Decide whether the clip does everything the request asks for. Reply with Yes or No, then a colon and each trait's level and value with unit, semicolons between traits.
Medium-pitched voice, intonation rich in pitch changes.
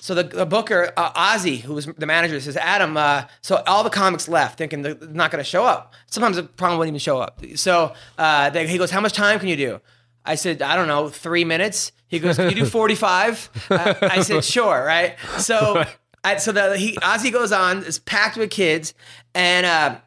No: medium, 175 Hz; average, 4.0 semitones